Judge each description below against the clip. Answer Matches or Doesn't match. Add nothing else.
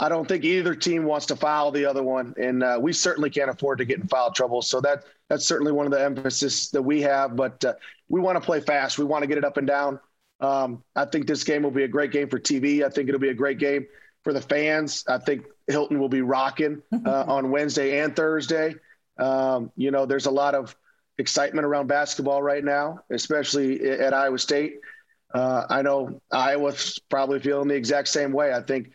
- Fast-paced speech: Matches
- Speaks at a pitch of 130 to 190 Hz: Matches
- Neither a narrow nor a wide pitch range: Doesn't match